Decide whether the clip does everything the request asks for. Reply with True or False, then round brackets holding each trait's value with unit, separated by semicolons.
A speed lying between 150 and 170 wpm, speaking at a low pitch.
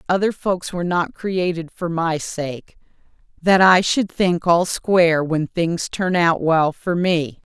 False (165 wpm; 175 Hz)